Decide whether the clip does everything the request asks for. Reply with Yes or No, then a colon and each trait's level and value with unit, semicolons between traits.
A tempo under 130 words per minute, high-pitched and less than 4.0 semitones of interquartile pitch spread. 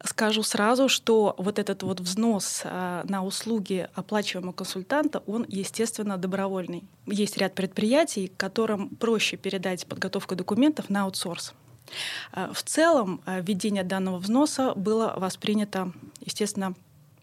Yes: slow, 110 wpm; high, 195 Hz; average, 2.7 semitones